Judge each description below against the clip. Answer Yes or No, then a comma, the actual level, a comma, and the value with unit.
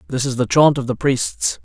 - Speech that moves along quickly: Yes, fast, 255 wpm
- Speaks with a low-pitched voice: Yes, low, 120 Hz